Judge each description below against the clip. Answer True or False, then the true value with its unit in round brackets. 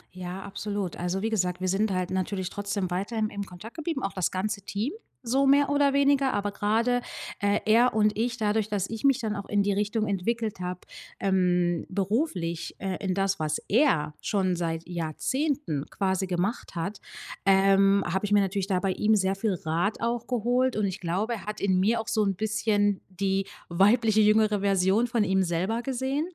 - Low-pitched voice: False (200 Hz)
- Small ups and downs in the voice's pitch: False (3.0 semitones)